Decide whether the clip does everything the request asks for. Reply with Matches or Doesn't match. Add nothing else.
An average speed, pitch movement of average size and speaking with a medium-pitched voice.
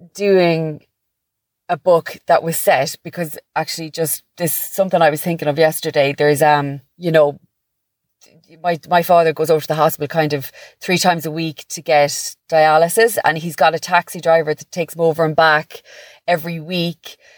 Doesn't match